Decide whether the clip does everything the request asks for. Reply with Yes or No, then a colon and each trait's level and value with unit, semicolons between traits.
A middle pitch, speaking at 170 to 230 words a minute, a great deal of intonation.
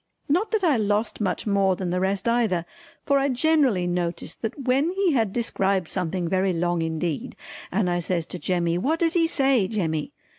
No: high, 195 Hz; average, 190 wpm; wide, 7.3 semitones